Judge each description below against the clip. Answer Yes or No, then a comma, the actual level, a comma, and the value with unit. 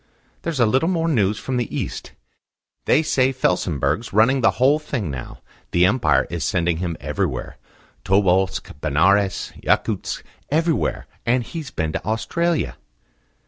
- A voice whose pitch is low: Yes, low, 110 Hz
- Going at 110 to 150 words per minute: Yes, average, 140 wpm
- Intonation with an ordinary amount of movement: No, wide, 7.0 semitones